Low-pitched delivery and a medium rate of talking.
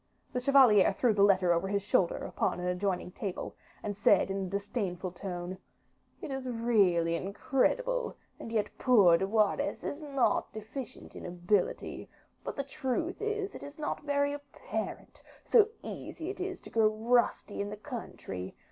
No: high, 215 Hz; average, 165 wpm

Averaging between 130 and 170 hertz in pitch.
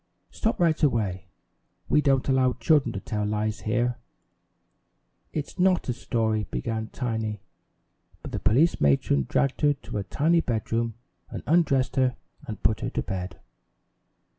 No: low, 120 Hz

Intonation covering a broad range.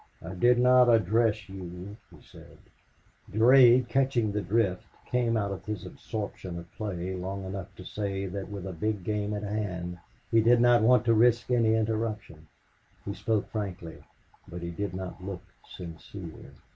No: average, 3.6 semitones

